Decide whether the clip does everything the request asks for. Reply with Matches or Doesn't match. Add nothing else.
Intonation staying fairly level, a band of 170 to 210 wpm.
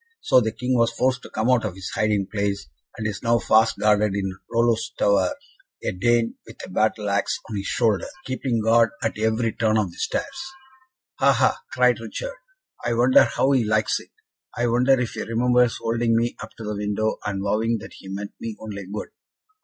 Matches